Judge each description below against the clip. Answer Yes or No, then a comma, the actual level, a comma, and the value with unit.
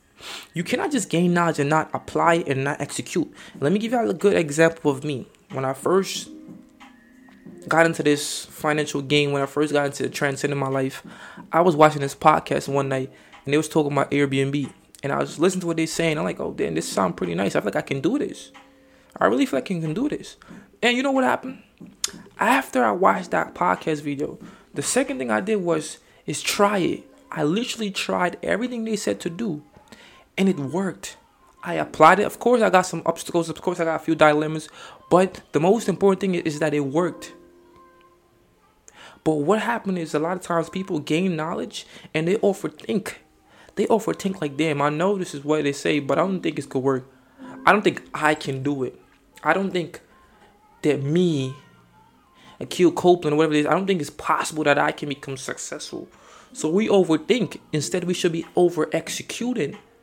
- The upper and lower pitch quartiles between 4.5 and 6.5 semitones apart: Yes, average, 4.8 semitones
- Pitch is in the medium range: Yes, medium, 165 Hz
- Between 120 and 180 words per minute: No, fast, 205 wpm